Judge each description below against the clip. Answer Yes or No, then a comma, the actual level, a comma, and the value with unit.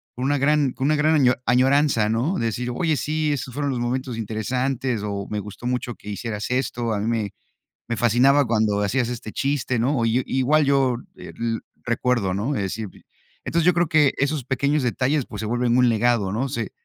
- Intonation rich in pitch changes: No, average, 3.5 semitones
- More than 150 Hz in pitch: No, low, 125 Hz